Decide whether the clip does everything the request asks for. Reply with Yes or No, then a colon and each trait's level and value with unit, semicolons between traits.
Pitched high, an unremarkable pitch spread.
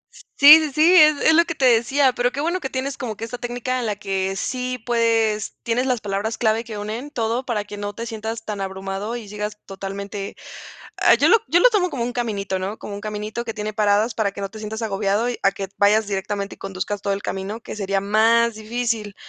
Yes: high, 220 Hz; average, 3.2 semitones